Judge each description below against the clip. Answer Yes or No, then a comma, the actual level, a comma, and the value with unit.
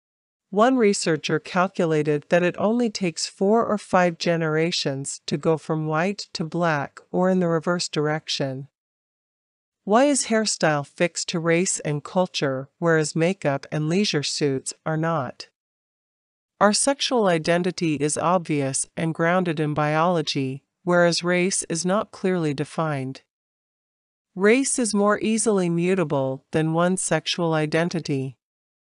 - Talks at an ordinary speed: No, slow, 125 wpm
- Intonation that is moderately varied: Yes, average, 3.4 semitones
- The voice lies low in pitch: No, medium, 170 Hz